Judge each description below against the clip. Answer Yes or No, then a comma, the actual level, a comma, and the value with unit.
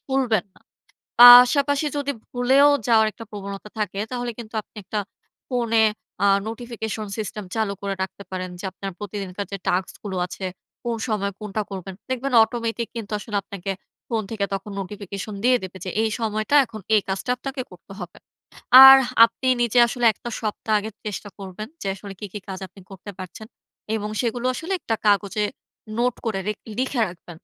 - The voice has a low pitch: No, high, 215 Hz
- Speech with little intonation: No, average, 3.3 semitones